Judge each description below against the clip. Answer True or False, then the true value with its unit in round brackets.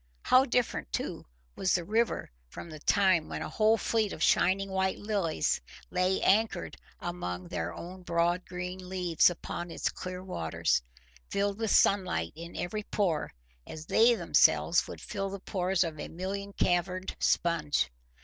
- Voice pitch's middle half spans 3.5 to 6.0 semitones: False (2.8 semitones)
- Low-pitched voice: False (185 Hz)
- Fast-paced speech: False (155 wpm)